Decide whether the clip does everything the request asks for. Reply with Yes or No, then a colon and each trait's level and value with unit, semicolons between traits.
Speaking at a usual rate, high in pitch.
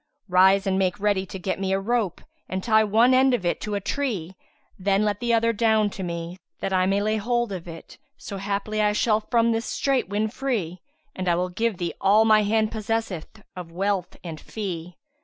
No: fast, 215 wpm; high, 205 Hz